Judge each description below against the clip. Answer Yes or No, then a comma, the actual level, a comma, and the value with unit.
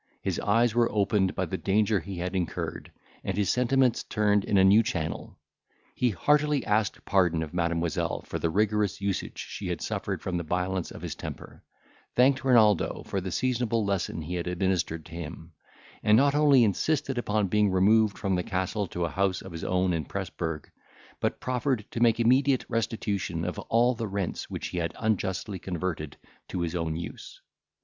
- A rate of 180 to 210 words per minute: Yes, average, 185 wpm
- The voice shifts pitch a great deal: No, average, 4.4 semitones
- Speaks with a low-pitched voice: Yes, low, 100 Hz